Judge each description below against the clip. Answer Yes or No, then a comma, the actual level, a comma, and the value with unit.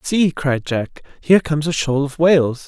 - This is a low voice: No, medium, 150 Hz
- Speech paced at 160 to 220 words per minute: Yes, average, 200 wpm